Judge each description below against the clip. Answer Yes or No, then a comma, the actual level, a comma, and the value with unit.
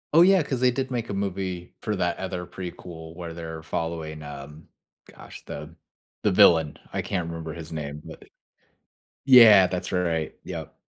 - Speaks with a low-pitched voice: Yes, very low, 85 Hz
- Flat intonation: No, average, 3.3 semitones